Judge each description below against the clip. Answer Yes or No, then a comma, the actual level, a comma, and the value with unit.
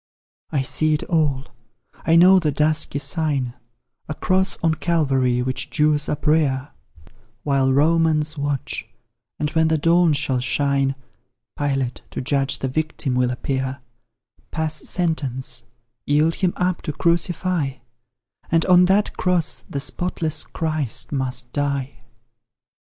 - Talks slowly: Yes, slow, 125 wpm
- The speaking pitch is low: No, medium, 150 Hz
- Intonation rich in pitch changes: No, average, 3.2 semitones